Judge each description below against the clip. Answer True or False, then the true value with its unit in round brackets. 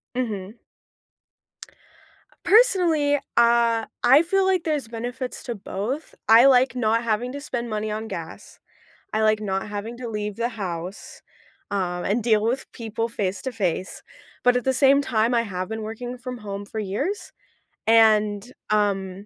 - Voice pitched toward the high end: True (225 Hz)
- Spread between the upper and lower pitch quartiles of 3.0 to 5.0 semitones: True (3.3 semitones)